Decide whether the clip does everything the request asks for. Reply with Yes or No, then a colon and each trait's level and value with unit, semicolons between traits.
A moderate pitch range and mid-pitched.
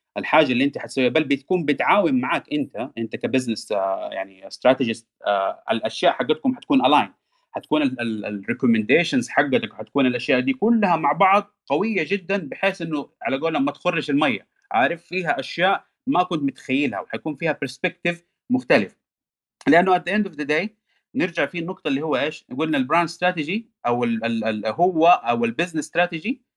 No: wide, 7.5 semitones; medium, 175 Hz